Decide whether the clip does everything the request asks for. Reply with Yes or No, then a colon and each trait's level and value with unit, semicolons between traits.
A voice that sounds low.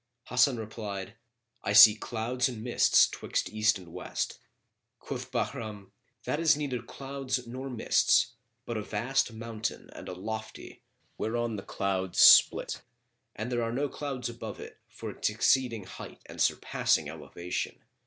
Yes: low, 115 Hz